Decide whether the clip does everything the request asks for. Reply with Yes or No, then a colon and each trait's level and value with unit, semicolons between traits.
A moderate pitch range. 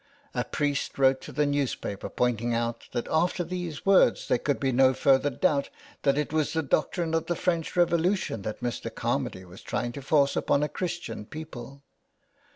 Yes: average, 4.3 semitones